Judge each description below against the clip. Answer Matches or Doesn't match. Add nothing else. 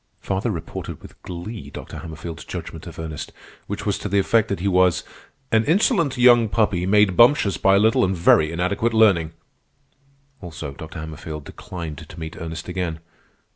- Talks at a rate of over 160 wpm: Matches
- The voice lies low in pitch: Matches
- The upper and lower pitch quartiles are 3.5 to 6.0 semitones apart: Matches